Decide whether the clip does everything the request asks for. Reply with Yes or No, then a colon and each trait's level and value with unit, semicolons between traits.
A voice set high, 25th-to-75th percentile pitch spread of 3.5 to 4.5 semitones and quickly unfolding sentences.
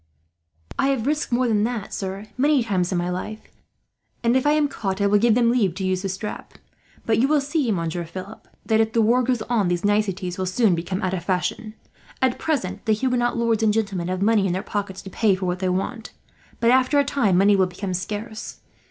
Yes: high, 210 Hz; average, 4.2 semitones; fast, 230 wpm